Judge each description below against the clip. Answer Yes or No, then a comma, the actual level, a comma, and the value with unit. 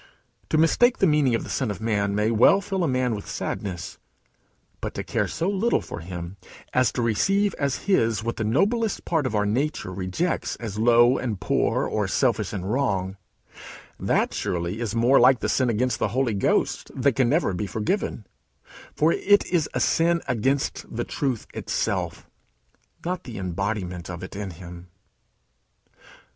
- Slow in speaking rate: No, average, 175 wpm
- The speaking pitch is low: Yes, low, 120 Hz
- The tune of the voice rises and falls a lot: Yes, wide, 6.7 semitones